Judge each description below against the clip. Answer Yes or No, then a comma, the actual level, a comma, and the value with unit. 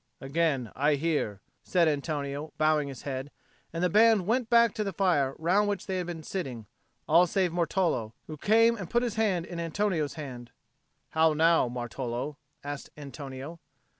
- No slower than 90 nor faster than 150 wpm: No, average, 165 wpm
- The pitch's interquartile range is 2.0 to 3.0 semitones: No, average, 5.0 semitones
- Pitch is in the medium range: Yes, medium, 160 Hz